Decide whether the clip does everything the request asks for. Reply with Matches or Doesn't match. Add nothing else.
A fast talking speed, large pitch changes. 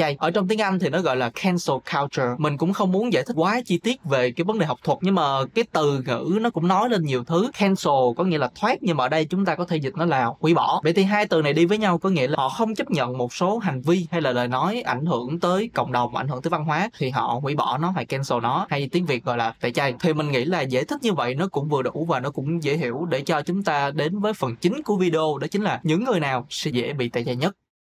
Matches